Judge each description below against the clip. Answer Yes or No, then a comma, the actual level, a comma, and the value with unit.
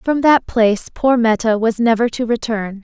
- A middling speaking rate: Yes, average, 190 wpm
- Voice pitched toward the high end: Yes, high, 230 Hz